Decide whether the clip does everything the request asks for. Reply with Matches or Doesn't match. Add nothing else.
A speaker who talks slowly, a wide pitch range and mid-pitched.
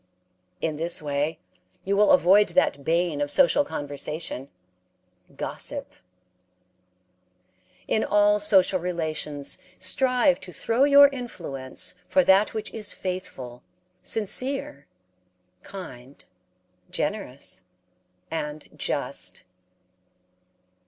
Matches